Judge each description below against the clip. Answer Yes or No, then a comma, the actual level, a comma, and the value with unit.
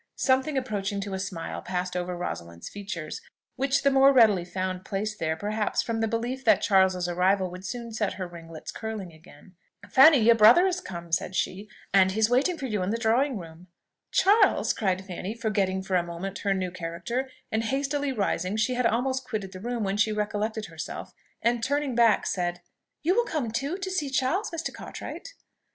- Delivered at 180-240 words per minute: Yes, average, 195 wpm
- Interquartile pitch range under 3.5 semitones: No, wide, 5.6 semitones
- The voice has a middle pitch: No, high, 210 Hz